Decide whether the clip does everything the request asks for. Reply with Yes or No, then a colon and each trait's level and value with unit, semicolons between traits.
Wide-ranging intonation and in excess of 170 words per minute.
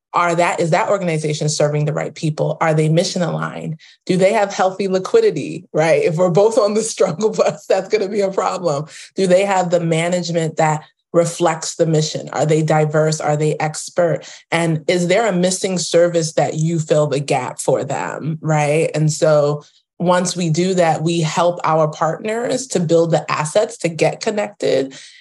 No: average, 3.0 semitones; average, 185 wpm